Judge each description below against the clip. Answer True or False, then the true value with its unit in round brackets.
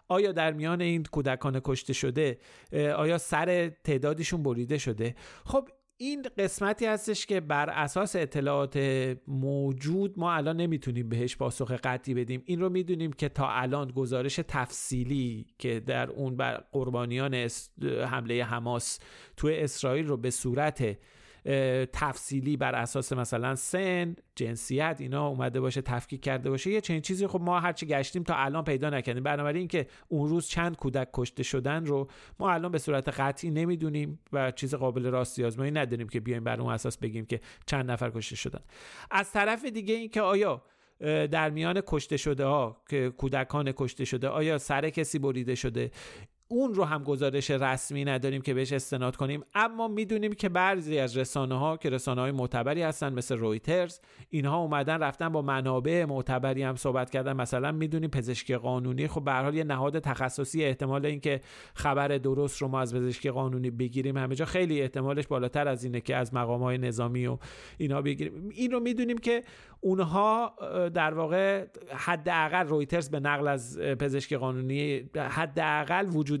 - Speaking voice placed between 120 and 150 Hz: True (140 Hz)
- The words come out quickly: True (160 wpm)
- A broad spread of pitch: False (3.8 semitones)